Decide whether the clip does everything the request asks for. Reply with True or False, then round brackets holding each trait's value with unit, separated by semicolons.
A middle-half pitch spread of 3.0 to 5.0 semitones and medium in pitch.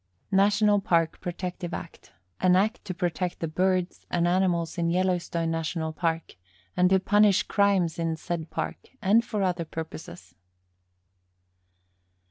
False (2.4 semitones; 180 Hz)